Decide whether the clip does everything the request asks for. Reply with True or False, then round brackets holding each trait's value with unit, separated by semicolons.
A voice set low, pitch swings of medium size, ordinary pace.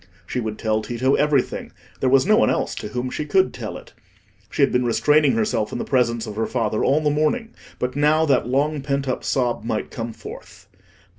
False (130 Hz; 4.5 semitones; 215 wpm)